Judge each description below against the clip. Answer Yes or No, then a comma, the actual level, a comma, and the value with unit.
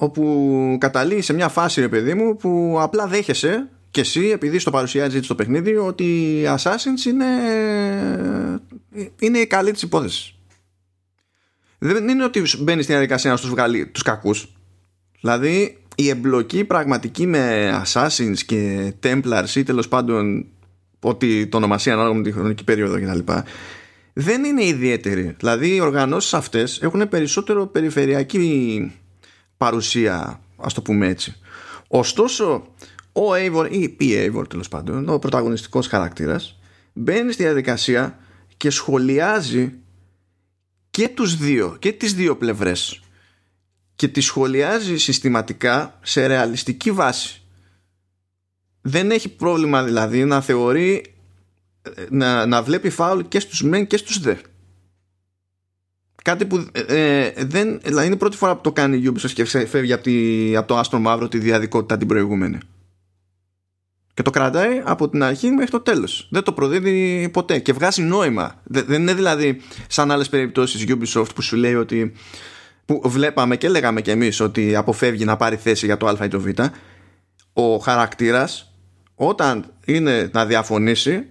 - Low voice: Yes, low, 125 Hz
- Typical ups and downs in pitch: No, wide, 7.7 semitones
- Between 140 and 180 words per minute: Yes, average, 145 wpm